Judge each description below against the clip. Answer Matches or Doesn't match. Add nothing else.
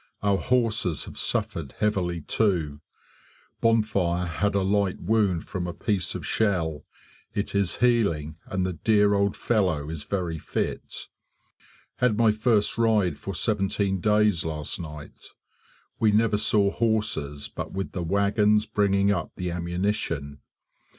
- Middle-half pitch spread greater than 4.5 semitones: Doesn't match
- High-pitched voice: Doesn't match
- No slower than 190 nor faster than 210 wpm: Doesn't match